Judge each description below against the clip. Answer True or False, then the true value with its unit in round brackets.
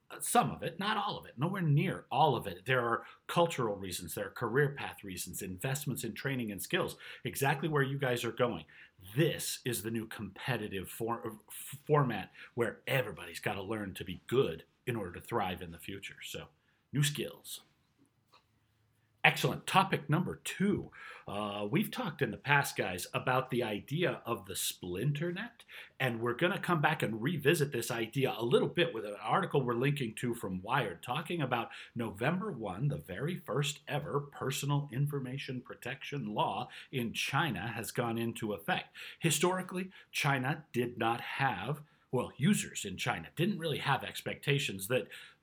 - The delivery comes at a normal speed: True (170 wpm)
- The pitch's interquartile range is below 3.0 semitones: False (4.5 semitones)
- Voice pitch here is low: True (130 Hz)